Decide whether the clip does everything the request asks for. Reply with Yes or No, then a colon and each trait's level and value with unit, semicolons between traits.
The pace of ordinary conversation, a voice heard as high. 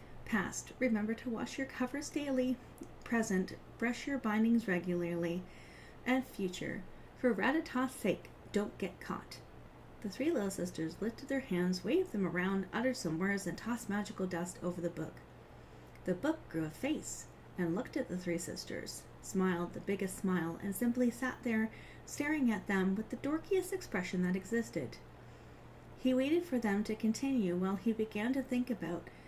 Yes: average, 165 wpm; high, 215 Hz